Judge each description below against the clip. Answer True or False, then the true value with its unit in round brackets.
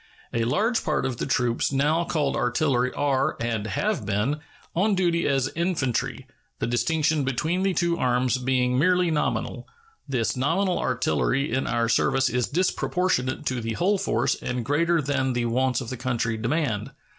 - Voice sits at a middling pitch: False (130 Hz)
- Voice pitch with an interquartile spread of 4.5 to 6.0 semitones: True (5.2 semitones)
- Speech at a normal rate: True (165 wpm)